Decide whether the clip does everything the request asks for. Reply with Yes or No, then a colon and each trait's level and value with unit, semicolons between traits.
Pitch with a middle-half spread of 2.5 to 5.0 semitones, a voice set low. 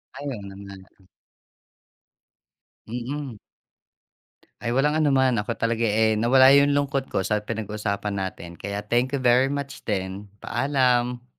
Yes: average, 4.4 semitones; low, 120 Hz